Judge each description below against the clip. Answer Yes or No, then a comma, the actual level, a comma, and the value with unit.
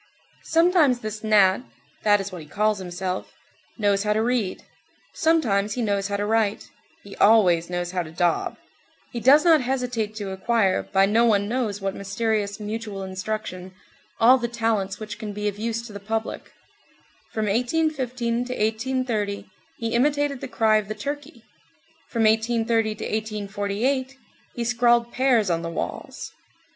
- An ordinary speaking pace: Yes, average, 155 wpm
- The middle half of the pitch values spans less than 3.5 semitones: Yes, average, 3.0 semitones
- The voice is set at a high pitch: Yes, high, 215 Hz